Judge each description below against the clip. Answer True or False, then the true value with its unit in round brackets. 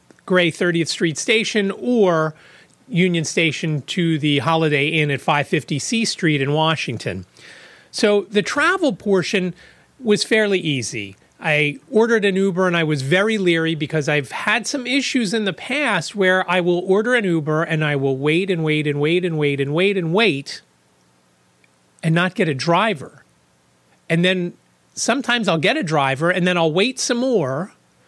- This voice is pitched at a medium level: True (170 Hz)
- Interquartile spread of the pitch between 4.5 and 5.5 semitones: True (5.1 semitones)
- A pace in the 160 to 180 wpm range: True (175 wpm)